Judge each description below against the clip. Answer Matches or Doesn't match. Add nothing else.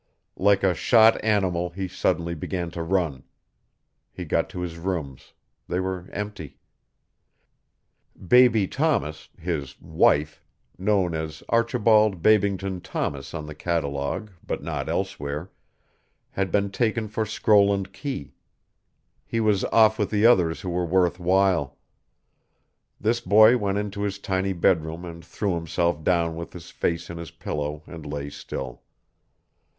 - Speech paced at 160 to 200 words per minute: Doesn't match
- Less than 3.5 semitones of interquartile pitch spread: Doesn't match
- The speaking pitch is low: Matches